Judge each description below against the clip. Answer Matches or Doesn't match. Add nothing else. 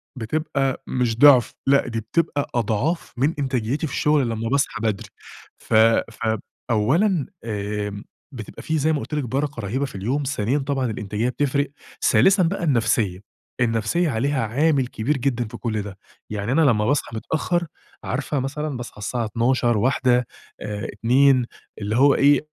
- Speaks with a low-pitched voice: Matches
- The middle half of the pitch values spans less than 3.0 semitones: Doesn't match